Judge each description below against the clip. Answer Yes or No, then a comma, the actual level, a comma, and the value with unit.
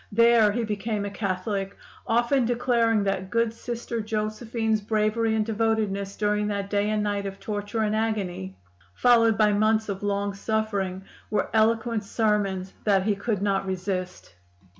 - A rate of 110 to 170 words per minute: Yes, average, 150 wpm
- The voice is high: Yes, high, 210 Hz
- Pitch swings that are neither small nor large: No, narrow, 2.0 semitones